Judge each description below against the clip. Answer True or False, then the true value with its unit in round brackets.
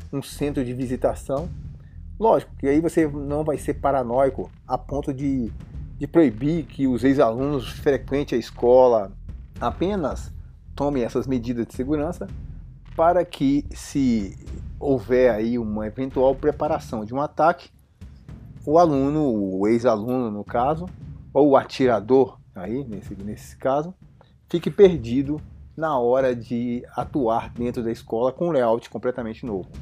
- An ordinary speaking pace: True (135 wpm)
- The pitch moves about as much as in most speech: True (4.1 semitones)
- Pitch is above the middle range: False (130 Hz)